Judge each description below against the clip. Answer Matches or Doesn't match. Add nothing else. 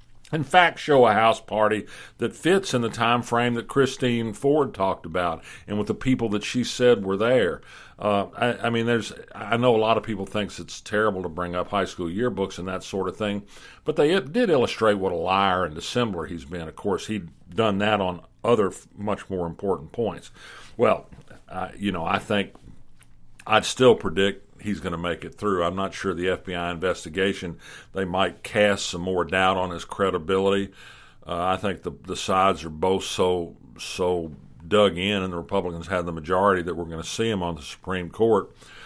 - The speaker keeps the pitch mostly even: Doesn't match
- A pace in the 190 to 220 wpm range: Matches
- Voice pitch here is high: Doesn't match